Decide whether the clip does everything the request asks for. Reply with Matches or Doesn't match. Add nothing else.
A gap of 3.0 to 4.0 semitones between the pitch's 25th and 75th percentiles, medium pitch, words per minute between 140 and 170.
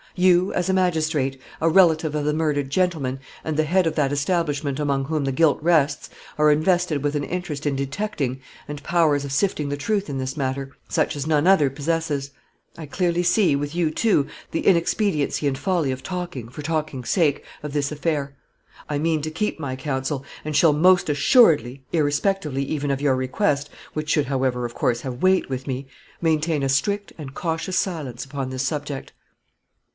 Doesn't match